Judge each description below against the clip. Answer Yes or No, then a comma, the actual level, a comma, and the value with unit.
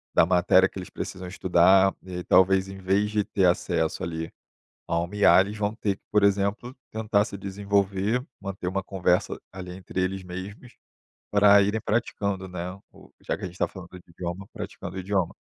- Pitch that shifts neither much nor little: No, narrow, 2.1 semitones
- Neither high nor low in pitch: No, very low, 95 Hz